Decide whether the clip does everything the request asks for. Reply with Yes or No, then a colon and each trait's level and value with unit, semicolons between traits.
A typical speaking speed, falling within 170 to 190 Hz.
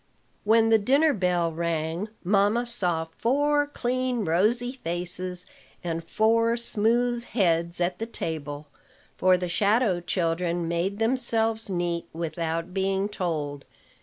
No: slow, 120 wpm; medium, 185 Hz